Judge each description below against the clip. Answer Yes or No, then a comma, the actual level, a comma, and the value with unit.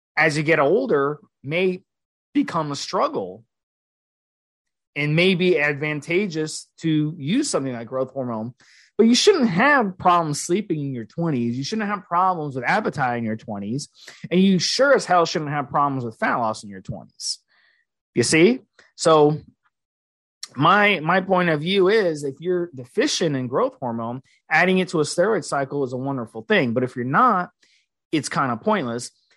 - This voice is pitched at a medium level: Yes, medium, 155 Hz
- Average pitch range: No, wide, 6.1 semitones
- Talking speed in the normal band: Yes, average, 170 wpm